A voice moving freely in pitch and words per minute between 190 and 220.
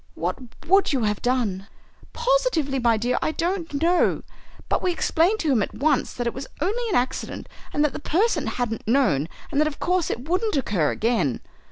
Yes: wide, 6.7 semitones; average, 195 wpm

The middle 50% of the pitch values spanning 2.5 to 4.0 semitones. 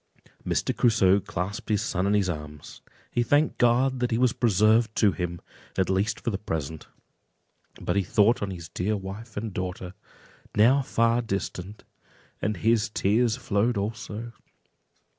Yes: average, 3.5 semitones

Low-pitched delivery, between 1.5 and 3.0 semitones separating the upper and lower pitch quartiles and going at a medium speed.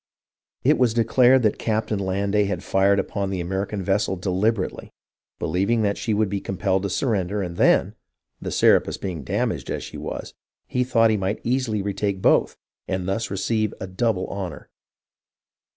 Yes: low, 100 Hz; narrow, 2.5 semitones; average, 170 wpm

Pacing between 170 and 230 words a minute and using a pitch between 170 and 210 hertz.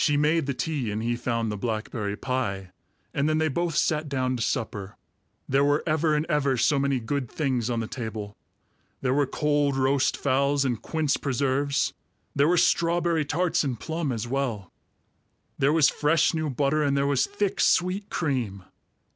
No: average, 180 wpm; medium, 140 Hz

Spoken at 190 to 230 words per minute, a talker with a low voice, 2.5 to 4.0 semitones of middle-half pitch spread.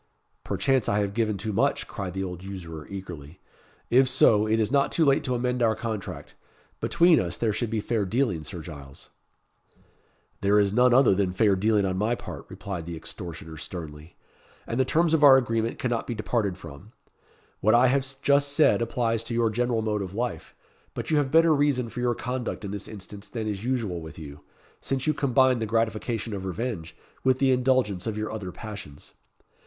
No: average, 195 wpm; low, 110 Hz; average, 4.6 semitones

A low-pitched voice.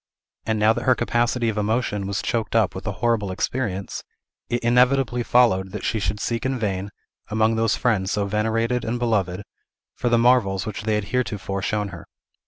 Yes: low, 110 Hz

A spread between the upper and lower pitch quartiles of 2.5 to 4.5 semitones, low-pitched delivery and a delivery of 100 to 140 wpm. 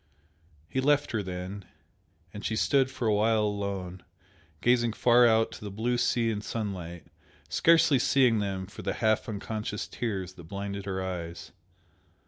No: average, 3.6 semitones; low, 105 Hz; average, 155 wpm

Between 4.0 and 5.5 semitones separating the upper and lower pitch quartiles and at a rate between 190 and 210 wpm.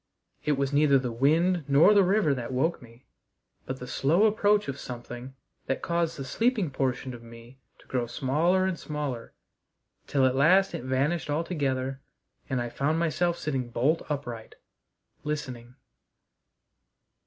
No: average, 4.6 semitones; average, 150 wpm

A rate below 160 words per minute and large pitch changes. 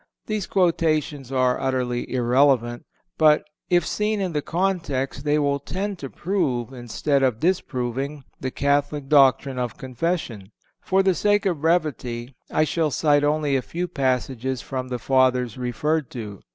No: average, 150 wpm; average, 4.1 semitones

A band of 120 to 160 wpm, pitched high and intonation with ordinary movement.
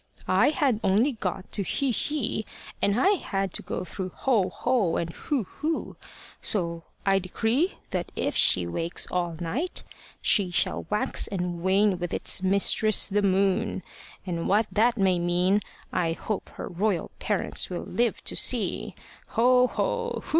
Yes: average, 155 wpm; high, 200 Hz; average, 4.3 semitones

